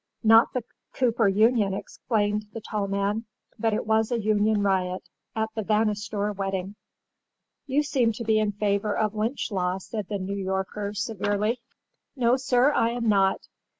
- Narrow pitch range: Yes, narrow, 2.2 semitones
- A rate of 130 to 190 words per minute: Yes, average, 150 wpm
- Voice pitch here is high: Yes, high, 210 Hz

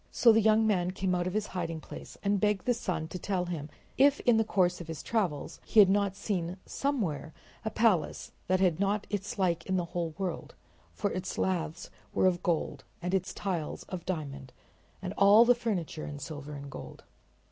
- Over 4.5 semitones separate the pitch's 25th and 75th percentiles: No, average, 3.5 semitones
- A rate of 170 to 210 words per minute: Yes, average, 200 wpm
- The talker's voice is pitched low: No, medium, 185 Hz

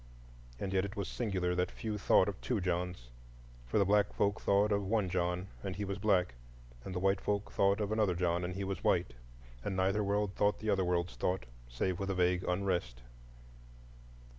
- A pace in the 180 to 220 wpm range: Yes, average, 195 wpm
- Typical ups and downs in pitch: No, narrow, 2.2 semitones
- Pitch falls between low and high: No, very low, 95 Hz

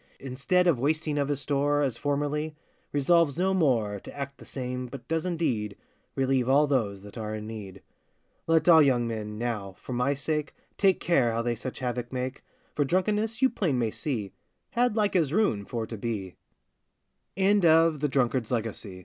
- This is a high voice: No, medium, 140 Hz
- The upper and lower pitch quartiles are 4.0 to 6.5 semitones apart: Yes, average, 5.1 semitones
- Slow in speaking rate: No, average, 160 wpm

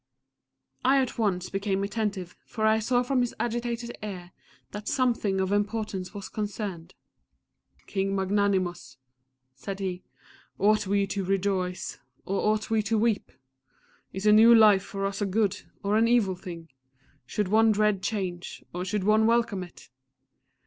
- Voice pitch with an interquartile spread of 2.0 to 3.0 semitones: Yes, narrow, 2.4 semitones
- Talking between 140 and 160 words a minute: Yes, average, 150 wpm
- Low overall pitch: No, high, 205 Hz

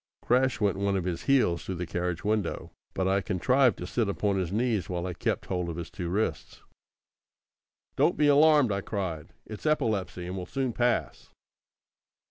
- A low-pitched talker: Yes, low, 100 Hz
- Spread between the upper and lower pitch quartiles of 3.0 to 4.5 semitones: No, average, 5.3 semitones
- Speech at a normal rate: Yes, average, 180 wpm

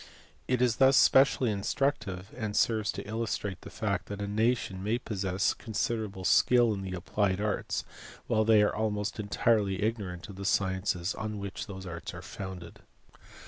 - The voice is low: Yes, low, 105 Hz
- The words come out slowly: No, average, 170 wpm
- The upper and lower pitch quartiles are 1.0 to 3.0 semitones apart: Yes, average, 2.7 semitones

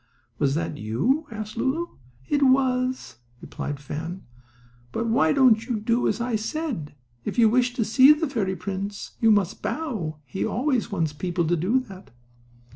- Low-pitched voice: No, high, 220 Hz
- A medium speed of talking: Yes, average, 165 wpm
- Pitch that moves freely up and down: Yes, wide, 6.4 semitones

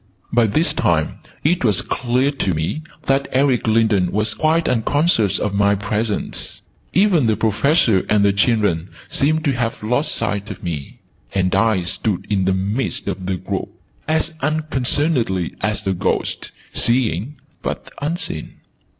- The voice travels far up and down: Yes, wide, 6.0 semitones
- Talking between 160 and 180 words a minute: No, average, 150 wpm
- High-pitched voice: No, low, 110 Hz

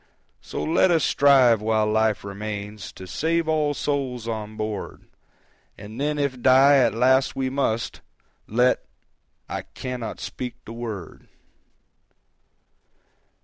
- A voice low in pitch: Yes, low, 125 Hz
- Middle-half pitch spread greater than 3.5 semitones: Yes, average, 4.3 semitones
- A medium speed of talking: No, slow, 120 wpm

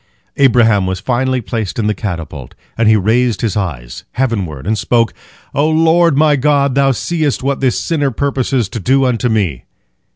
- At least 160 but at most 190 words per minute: Yes, average, 170 wpm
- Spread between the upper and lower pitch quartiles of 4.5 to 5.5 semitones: Yes, average, 4.8 semitones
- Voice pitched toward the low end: Yes, low, 120 Hz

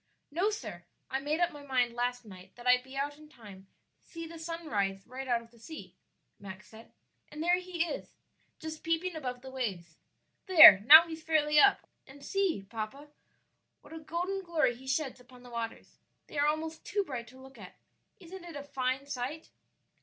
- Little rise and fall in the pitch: No, average, 5.0 semitones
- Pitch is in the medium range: No, very high, 280 Hz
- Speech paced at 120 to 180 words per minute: No, average, 200 wpm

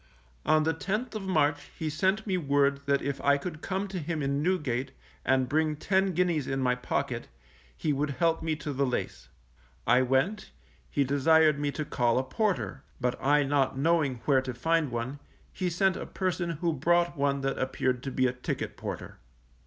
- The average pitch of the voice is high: No, medium, 145 Hz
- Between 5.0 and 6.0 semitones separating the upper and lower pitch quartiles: No, average, 4.0 semitones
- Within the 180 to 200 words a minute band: Yes, average, 195 wpm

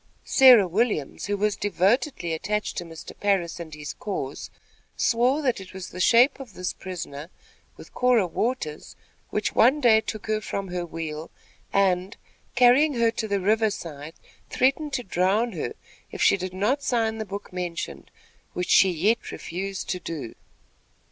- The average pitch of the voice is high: Yes, high, 200 Hz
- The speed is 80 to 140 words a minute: No, average, 160 wpm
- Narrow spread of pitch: No, average, 4.8 semitones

